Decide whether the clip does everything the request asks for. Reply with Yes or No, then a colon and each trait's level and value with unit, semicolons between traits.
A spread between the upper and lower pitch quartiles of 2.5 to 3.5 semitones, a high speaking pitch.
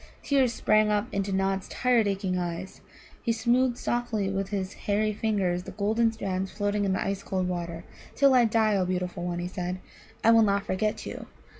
Yes: average, 2.9 semitones; high, 200 Hz